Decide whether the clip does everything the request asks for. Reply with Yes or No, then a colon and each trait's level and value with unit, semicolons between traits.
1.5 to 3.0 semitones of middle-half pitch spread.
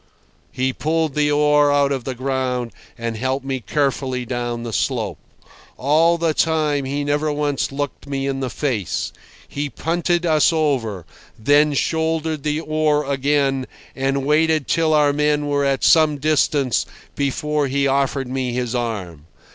Yes: narrow, 2.5 semitones